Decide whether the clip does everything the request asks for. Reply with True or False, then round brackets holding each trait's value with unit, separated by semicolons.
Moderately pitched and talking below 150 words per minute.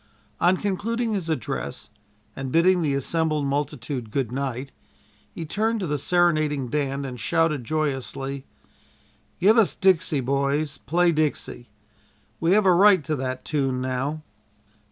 True (150 Hz; 135 wpm)